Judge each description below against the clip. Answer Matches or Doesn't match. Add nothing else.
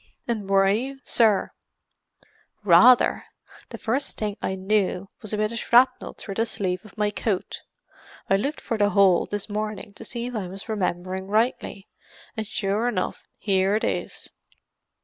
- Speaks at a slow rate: Doesn't match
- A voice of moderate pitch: Doesn't match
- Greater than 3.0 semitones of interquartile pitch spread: Doesn't match